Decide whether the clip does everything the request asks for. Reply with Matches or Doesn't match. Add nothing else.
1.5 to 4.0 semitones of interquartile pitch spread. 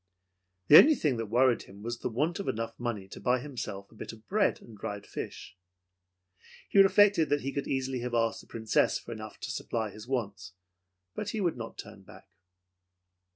Doesn't match